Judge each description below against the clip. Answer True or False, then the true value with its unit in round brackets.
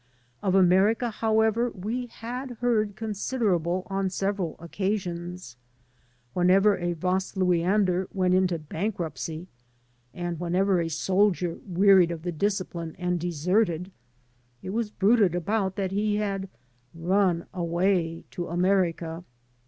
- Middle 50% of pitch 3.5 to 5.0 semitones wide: False (2.8 semitones)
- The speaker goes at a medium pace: False (120 wpm)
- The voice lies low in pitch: False (185 Hz)